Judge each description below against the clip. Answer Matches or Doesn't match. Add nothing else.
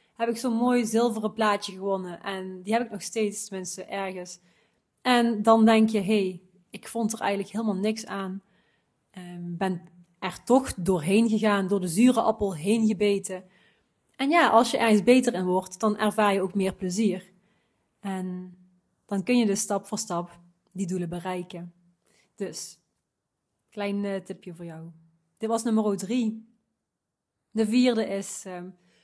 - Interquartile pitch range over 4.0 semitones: Doesn't match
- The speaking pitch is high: Matches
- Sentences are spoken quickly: Doesn't match